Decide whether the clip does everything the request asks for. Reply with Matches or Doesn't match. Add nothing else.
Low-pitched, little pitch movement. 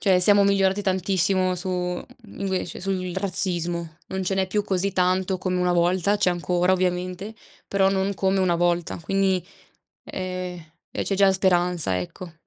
Doesn't match